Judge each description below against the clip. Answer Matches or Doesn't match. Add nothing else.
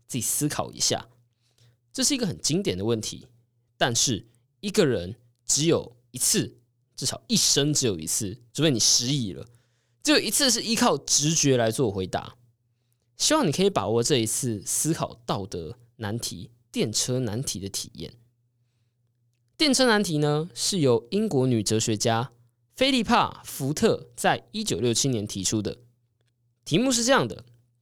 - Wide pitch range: Doesn't match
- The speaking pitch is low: Matches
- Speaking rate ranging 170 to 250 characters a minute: Matches